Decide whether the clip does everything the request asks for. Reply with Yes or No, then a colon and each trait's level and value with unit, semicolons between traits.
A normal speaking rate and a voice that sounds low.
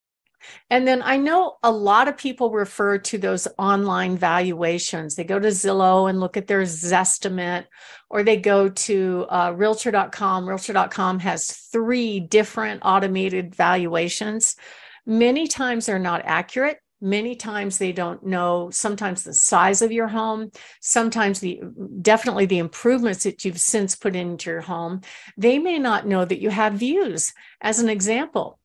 No: average, 155 wpm; high, 200 Hz